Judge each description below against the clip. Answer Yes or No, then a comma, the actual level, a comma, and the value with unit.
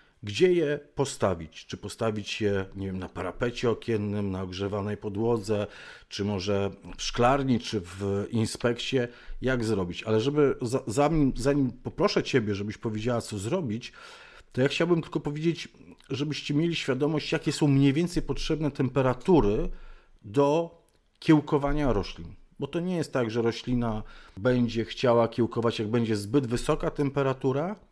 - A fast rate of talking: No, average, 145 wpm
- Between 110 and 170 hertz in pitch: Yes, low, 120 Hz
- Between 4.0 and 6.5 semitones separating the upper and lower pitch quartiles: Yes, average, 5.3 semitones